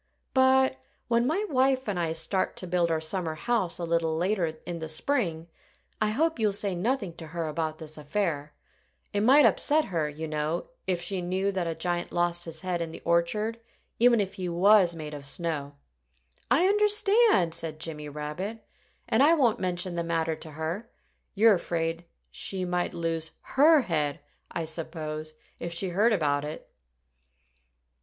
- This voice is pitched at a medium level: Yes, medium, 175 Hz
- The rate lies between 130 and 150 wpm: No, average, 170 wpm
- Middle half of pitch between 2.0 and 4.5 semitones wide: No, average, 4.9 semitones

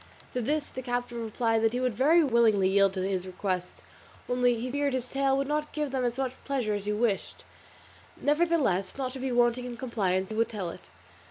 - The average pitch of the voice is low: No, high, 245 Hz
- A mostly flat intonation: No, average, 4.2 semitones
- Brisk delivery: Yes, fast, 210 wpm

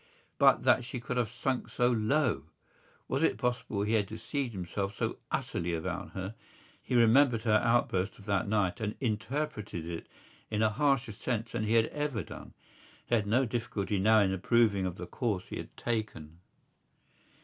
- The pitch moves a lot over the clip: No, average, 3.5 semitones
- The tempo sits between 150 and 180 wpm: Yes, average, 175 wpm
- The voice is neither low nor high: No, low, 110 Hz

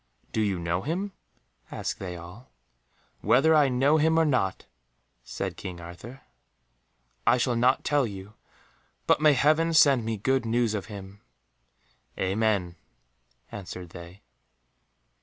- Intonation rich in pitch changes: Yes, wide, 6.5 semitones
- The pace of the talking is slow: Yes, slow, 130 wpm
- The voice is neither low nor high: No, low, 115 Hz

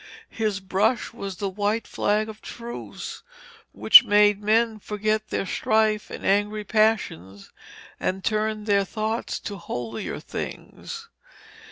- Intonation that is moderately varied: No, narrow, 1.6 semitones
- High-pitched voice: Yes, high, 210 Hz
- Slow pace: Yes, slow, 125 wpm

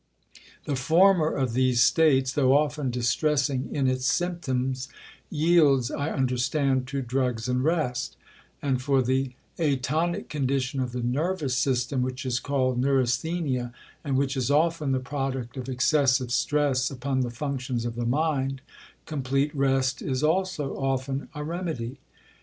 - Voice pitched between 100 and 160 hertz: Yes, low, 135 Hz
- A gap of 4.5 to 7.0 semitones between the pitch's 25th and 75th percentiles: No, narrow, 2.6 semitones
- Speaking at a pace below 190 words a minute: Yes, average, 140 wpm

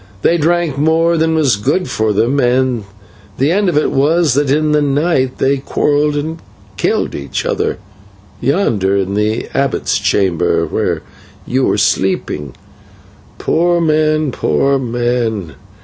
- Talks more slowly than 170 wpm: Yes, average, 140 wpm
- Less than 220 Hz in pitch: Yes, medium, 140 Hz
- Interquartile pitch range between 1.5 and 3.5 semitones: No, average, 5.2 semitones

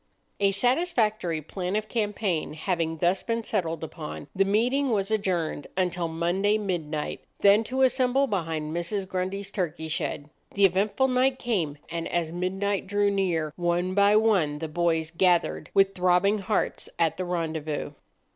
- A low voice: No, medium, 185 Hz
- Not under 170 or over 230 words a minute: No, average, 150 wpm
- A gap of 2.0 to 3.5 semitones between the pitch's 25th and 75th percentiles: No, average, 3.9 semitones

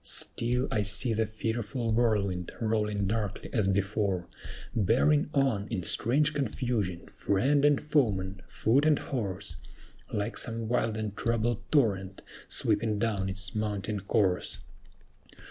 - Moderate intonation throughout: Yes, average, 3.3 semitones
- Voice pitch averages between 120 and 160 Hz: No, low, 110 Hz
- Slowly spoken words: Yes, slow, 125 wpm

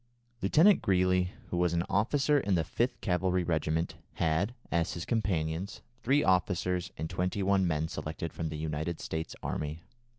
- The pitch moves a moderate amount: Yes, average, 3.4 semitones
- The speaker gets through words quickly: No, average, 160 wpm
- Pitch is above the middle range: No, very low, 90 Hz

